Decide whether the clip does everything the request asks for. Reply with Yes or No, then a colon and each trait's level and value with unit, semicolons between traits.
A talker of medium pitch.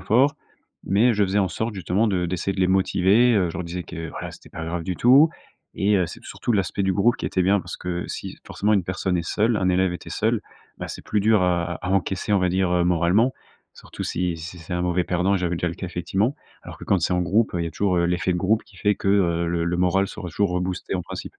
No: very low, 95 Hz